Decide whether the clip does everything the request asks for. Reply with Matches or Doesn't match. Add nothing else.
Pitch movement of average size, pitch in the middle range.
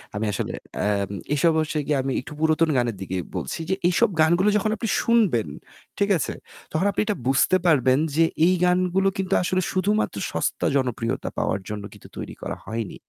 Doesn't match